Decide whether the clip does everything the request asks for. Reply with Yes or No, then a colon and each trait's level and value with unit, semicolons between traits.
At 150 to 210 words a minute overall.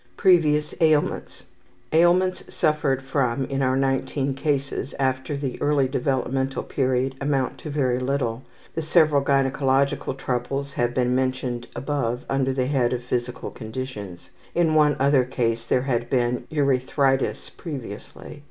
No: slow, 135 wpm